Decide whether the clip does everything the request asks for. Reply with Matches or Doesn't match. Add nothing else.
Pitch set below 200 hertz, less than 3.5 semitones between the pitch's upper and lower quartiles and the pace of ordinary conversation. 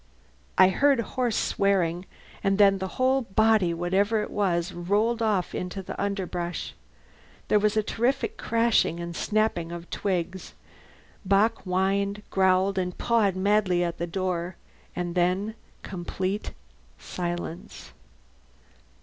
Doesn't match